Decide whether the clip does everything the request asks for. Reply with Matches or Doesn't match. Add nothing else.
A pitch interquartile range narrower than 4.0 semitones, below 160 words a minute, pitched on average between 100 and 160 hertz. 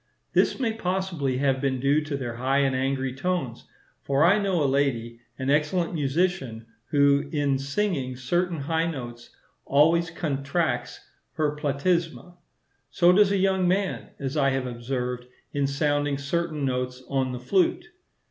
Doesn't match